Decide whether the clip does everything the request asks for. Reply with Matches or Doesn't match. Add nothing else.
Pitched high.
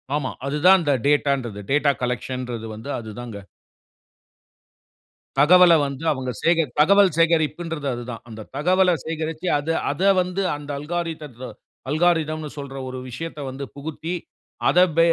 Doesn't match